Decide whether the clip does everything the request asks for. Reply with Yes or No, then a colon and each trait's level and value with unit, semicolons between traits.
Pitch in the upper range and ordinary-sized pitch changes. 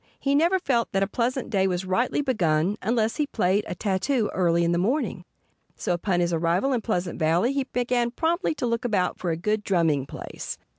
No: high, 210 Hz; wide, 6.0 semitones